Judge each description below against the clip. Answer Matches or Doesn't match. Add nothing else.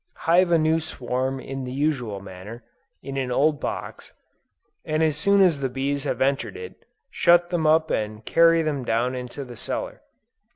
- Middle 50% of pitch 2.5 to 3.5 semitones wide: Doesn't match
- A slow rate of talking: Doesn't match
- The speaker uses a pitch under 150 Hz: Matches